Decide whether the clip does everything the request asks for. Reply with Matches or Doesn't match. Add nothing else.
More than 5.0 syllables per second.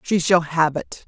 Doesn't match